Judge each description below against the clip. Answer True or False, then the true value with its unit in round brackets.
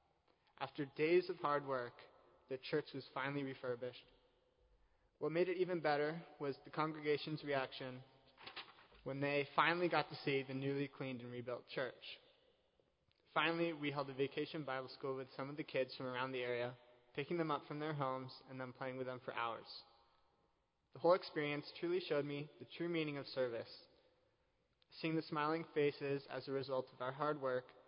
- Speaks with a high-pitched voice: False (140 Hz)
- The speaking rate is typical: True (175 wpm)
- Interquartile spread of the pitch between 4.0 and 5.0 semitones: False (3.0 semitones)